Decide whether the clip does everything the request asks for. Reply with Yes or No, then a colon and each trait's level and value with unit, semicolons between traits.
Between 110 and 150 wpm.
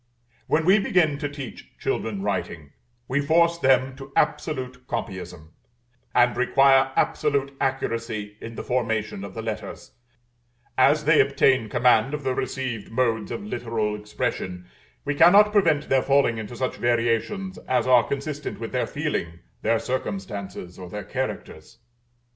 Yes: average, 140 wpm